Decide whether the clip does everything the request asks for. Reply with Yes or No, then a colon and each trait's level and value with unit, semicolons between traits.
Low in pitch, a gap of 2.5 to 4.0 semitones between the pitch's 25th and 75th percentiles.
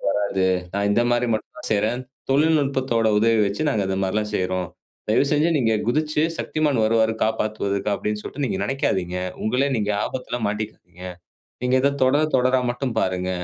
No: low, 110 Hz; average, 4.5 semitones